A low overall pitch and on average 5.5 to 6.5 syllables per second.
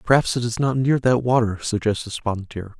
Yes: low, 115 Hz; 5.6 syllables/s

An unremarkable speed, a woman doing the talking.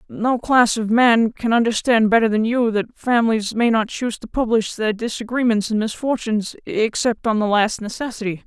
Yes: average, 175 wpm; female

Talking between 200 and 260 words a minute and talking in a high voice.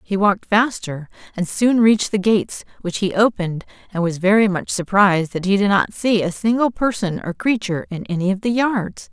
Yes: fast, 205 wpm; high, 200 Hz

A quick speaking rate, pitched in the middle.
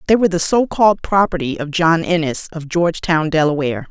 No: average, 185 wpm; medium, 170 Hz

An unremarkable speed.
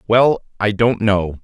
Yes: average, 170 wpm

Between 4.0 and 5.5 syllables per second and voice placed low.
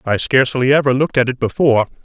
No: 7.3 syllables/s; low, 130 Hz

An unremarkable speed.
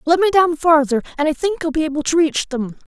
No: fast, 265 wpm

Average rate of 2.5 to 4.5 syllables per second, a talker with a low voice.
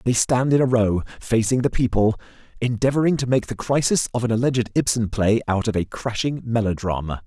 No: 5.7 syllables/s; low, 115 Hz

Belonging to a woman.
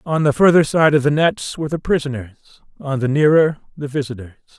No: male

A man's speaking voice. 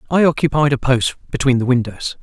Yes: male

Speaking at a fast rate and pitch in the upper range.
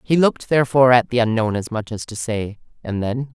No: fast, 230 wpm; low, 120 Hz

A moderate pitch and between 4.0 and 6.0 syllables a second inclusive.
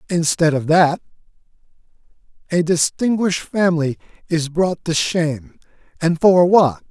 Yes: medium, 170 Hz; 4.5 syllables/s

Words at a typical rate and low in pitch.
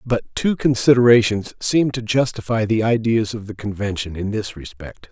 Yes: average, 165 wpm; low, 110 Hz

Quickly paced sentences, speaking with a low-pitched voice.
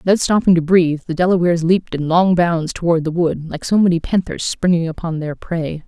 No: fast, 215 wpm; medium, 170 Hz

